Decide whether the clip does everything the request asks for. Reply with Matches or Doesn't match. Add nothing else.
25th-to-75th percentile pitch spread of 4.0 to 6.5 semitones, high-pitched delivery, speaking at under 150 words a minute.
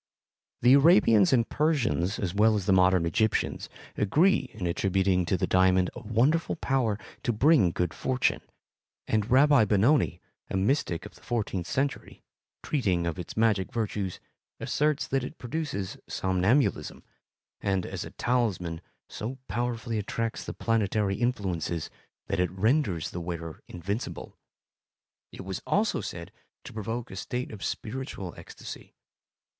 Doesn't match